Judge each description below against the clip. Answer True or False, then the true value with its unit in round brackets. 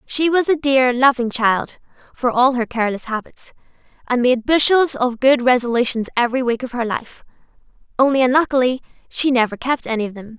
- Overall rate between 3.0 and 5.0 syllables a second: False (5.5 syllables/s)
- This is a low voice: False (250 Hz)